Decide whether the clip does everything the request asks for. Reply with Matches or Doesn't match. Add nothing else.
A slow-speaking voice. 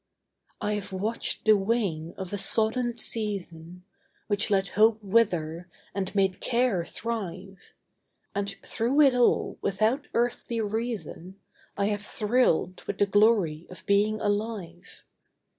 Matches